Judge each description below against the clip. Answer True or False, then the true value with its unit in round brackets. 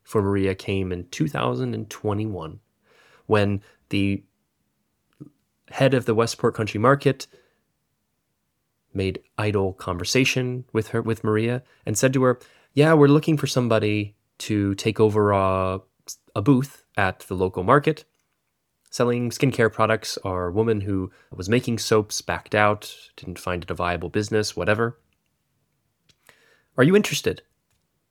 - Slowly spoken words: True (130 wpm)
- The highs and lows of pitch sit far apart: False (4.1 semitones)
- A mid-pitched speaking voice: False (110 Hz)